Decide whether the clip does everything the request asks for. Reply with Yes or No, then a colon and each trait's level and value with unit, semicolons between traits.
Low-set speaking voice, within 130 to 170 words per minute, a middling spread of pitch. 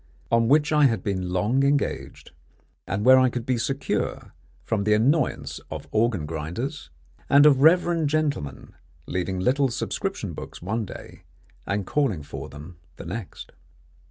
No: low, 115 Hz; average, 150 wpm; wide, 7.1 semitones